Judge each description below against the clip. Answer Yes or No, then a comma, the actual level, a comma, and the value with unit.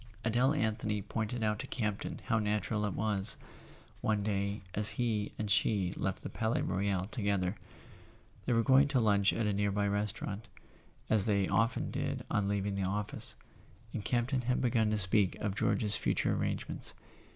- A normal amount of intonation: No, narrow, 2.0 semitones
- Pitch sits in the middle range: No, low, 105 Hz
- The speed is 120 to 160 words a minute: No, average, 180 wpm